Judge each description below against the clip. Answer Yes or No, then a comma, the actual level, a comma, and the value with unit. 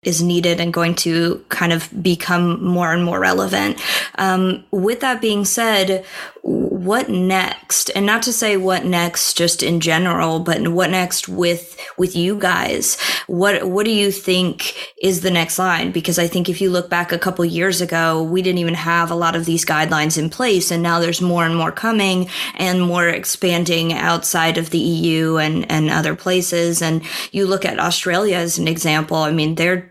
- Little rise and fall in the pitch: Yes, narrow, 1.9 semitones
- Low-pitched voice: No, medium, 175 Hz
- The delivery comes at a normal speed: Yes, average, 190 wpm